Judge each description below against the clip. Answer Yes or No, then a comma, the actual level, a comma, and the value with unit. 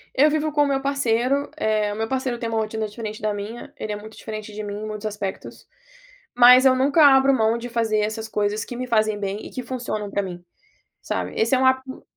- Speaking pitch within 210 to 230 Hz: Yes, high, 225 Hz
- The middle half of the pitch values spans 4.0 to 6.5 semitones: No, average, 3.5 semitones